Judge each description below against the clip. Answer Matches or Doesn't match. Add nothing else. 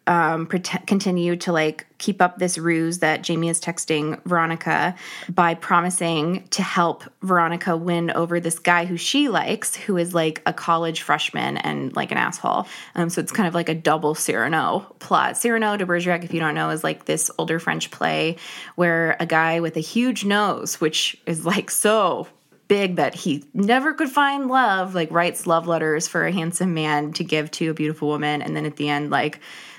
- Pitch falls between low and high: Matches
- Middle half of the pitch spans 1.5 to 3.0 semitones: Matches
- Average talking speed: Matches